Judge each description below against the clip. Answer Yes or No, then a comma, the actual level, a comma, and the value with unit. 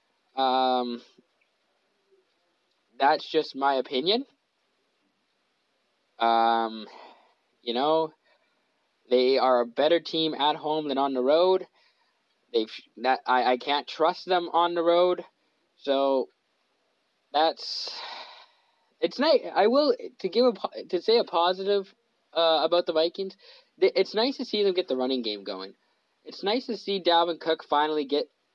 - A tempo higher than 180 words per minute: No, slow, 135 wpm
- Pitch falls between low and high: Yes, medium, 165 Hz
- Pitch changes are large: Yes, wide, 6.8 semitones